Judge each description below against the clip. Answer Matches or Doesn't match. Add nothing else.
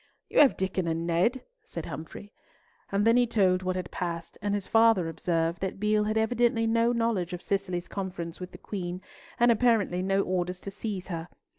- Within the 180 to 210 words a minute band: Matches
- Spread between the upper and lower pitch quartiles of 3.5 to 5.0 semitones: Matches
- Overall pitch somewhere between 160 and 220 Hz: Matches